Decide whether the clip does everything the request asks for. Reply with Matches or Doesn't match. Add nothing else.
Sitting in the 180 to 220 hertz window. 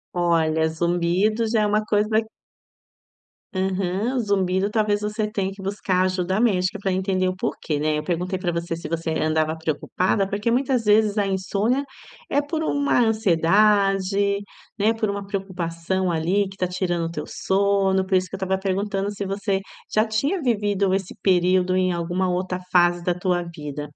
Matches